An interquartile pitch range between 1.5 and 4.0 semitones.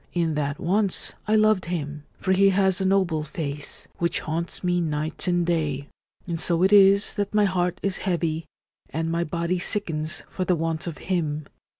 Yes: average, 3.2 semitones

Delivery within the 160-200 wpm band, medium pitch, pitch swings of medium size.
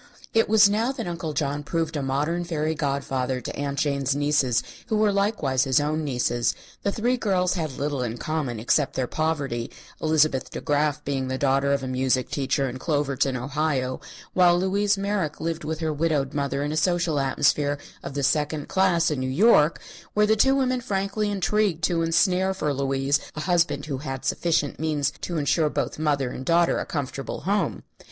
Yes: average, 190 wpm; medium, 150 Hz; average, 4.2 semitones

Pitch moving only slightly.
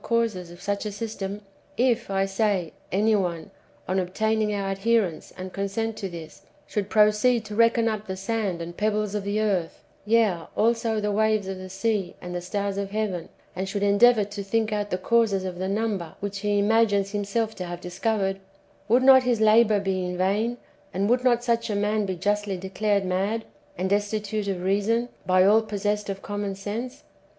Yes: narrow, 2.3 semitones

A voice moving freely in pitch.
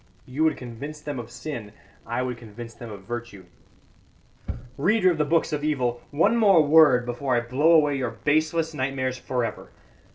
No: average, 4.3 semitones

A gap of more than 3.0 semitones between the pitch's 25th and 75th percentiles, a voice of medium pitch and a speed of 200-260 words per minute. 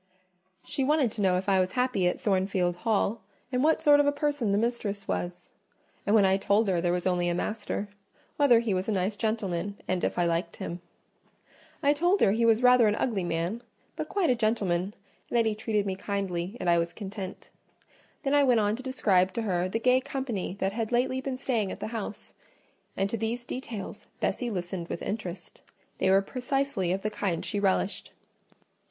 No: average, 4.5 semitones; high, 210 Hz; fast, 205 wpm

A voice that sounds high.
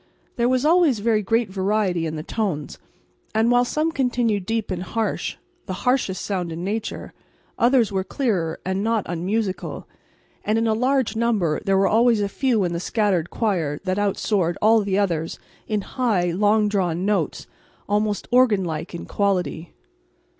Yes: high, 205 Hz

